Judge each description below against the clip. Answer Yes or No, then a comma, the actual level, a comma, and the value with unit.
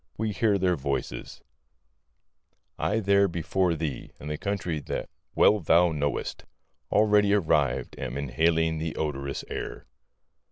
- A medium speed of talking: No, slow, 125 wpm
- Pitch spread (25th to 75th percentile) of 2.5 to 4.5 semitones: No, wide, 5.5 semitones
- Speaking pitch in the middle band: No, very low, 80 Hz